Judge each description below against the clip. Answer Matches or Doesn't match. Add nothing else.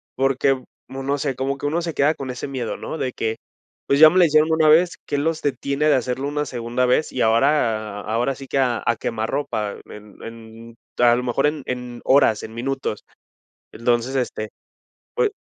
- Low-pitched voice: Matches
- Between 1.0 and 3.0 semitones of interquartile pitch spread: Doesn't match